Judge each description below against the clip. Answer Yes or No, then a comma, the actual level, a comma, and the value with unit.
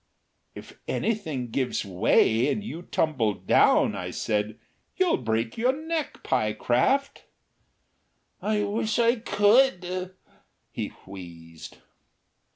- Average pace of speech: No, slow, 100 wpm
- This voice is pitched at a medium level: Yes, medium, 165 Hz